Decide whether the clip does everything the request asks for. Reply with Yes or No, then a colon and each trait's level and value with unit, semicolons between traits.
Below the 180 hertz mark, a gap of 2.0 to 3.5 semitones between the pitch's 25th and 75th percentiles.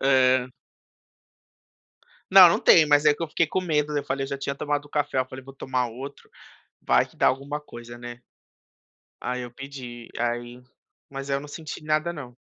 Yes: medium, 140 Hz; average, 2.9 semitones